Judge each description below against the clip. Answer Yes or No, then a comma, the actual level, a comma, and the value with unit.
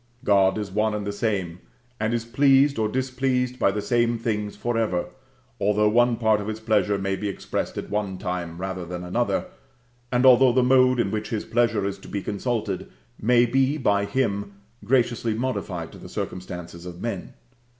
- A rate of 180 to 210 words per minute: Yes, average, 185 wpm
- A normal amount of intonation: Yes, average, 3.6 semitones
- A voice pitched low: Yes, low, 110 Hz